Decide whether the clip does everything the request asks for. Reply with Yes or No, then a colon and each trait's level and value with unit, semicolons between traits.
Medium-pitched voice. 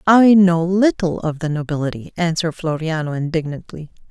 Yes: medium, 165 Hz